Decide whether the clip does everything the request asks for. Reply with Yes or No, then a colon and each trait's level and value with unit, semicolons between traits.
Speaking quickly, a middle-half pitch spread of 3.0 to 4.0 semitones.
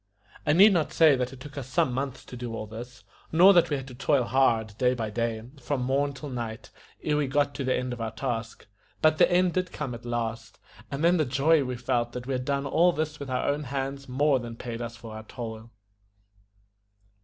Yes: fast, 235 wpm; average, 3.5 semitones